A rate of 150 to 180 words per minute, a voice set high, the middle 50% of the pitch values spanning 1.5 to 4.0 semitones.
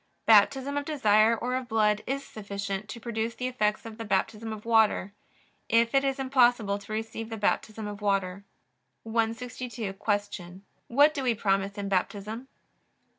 Yes: average, 160 wpm; high, 220 Hz; average, 2.9 semitones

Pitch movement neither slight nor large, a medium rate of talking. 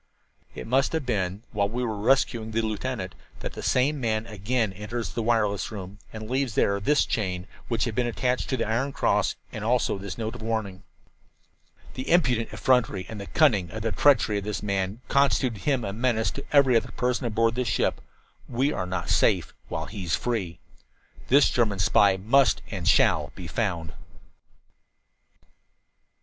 Yes: average, 3.8 semitones; average, 170 wpm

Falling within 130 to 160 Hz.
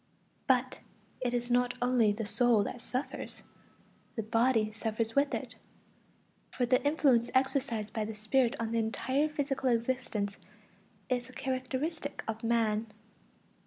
No: high, 245 Hz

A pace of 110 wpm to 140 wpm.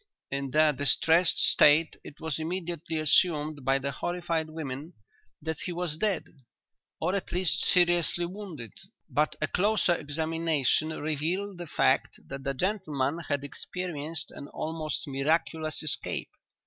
Yes: slow, 135 wpm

